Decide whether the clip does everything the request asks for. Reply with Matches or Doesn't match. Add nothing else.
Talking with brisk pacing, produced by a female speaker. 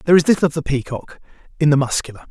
Doesn't match